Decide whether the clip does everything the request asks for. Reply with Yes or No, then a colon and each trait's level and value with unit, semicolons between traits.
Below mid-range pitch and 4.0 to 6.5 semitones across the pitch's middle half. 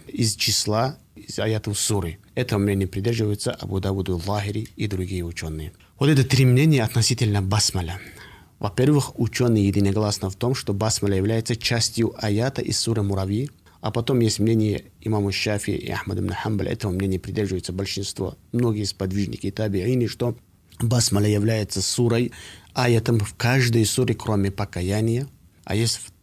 No: low, 105 Hz; average, 3.2 semitones